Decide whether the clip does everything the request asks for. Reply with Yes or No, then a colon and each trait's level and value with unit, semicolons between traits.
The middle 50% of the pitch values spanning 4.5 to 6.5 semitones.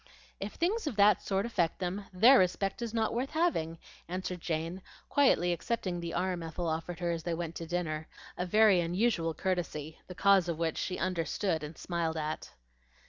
No: average, 3.3 semitones